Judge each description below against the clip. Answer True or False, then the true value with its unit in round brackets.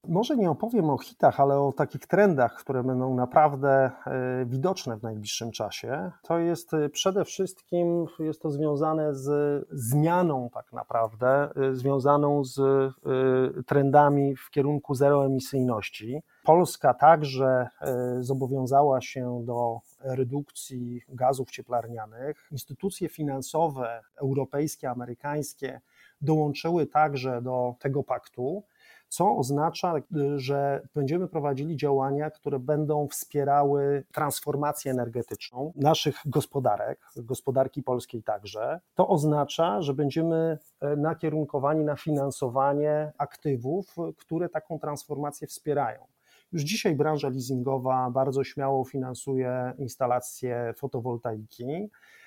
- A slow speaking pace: True (100 wpm)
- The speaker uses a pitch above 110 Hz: True (140 Hz)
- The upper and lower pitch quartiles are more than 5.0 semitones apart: False (2.8 semitones)